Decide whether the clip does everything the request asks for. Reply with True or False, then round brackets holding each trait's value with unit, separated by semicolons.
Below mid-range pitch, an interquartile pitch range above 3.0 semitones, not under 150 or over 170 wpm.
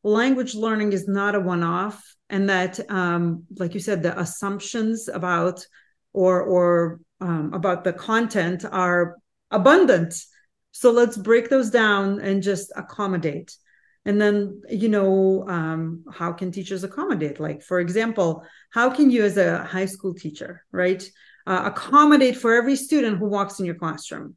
False (195 Hz; 3.4 semitones; 155 wpm)